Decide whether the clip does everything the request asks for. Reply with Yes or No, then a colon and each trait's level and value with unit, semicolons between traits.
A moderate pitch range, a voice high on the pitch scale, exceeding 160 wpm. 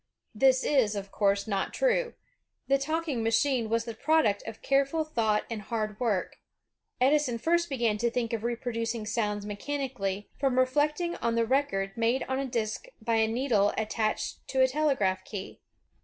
Yes: average, 4.2 semitones; high, 235 Hz; average, 170 wpm